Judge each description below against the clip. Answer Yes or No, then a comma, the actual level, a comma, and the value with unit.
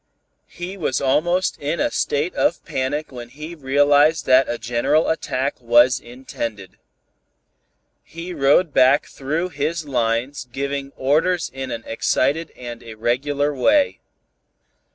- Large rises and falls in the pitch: No, average, 3.7 semitones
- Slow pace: Yes, slow, 125 wpm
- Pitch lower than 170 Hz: Yes, medium, 140 Hz